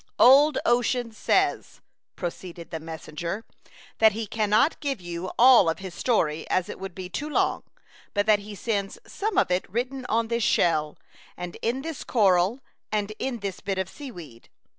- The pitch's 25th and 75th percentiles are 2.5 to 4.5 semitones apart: No, average, 5.3 semitones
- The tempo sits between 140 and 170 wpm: No, average, 185 wpm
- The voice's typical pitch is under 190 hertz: No, high, 205 Hz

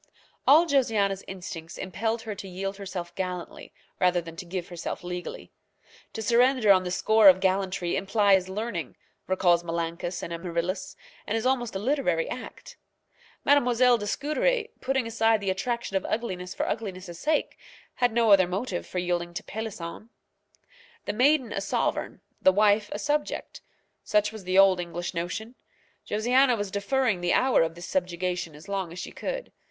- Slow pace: No, average, 165 wpm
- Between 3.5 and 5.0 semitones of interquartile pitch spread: Yes, average, 4.3 semitones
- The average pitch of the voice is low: No, high, 195 Hz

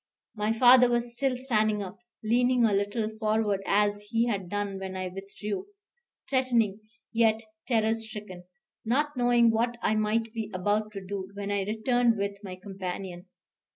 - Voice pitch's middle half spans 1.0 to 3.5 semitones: Yes, average, 2.9 semitones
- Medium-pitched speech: No, high, 215 Hz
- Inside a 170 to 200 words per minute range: No, average, 155 wpm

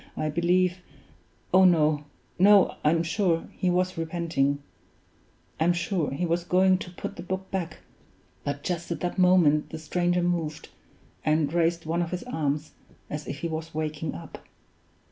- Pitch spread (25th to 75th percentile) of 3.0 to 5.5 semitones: No, narrow, 2.5 semitones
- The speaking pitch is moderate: Yes, medium, 170 Hz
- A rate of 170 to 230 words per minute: No, average, 160 wpm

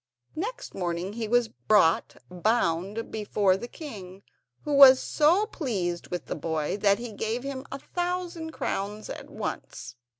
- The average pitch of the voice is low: No, high, 220 Hz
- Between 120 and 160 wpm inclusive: Yes, average, 145 wpm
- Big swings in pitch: Yes, wide, 6.9 semitones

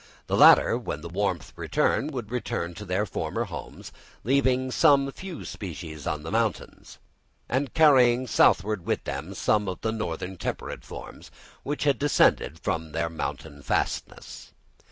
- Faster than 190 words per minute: No, average, 150 wpm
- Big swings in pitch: Yes, wide, 7.5 semitones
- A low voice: Yes, low, 105 Hz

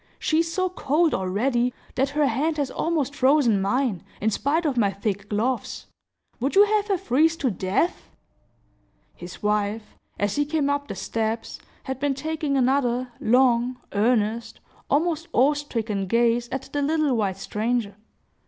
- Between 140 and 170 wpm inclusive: Yes, average, 155 wpm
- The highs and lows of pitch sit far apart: No, average, 5.0 semitones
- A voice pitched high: Yes, very high, 255 Hz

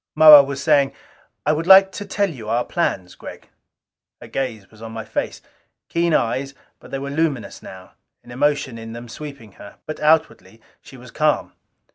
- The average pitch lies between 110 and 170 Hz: Yes, medium, 140 Hz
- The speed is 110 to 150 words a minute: No, average, 180 wpm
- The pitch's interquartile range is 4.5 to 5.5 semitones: Yes, average, 5.1 semitones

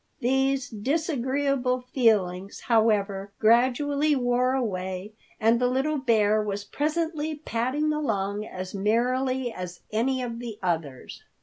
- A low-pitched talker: No, high, 240 Hz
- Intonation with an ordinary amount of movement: Yes, average, 4.5 semitones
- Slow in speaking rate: Yes, slow, 115 wpm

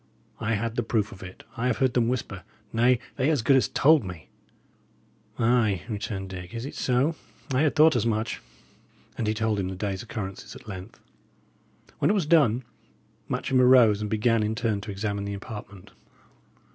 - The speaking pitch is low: Yes, low, 115 Hz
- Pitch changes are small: No, average, 3.7 semitones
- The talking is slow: No, average, 185 wpm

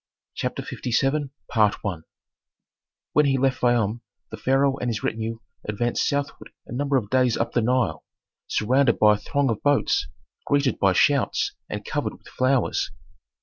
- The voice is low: Yes, low, 125 Hz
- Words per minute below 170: Yes, average, 145 wpm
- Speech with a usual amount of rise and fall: Yes, average, 3.4 semitones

